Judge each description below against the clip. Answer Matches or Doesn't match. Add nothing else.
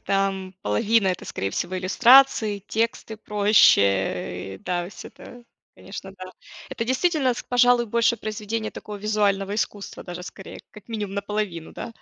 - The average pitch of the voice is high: Matches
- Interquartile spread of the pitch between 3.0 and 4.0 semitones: Matches